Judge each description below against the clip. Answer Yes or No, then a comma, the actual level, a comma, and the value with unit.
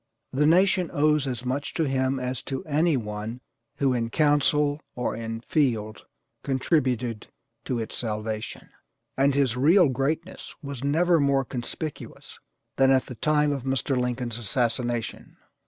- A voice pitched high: No, low, 135 Hz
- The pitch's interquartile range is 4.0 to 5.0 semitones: No, average, 3.6 semitones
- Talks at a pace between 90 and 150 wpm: Yes, average, 140 wpm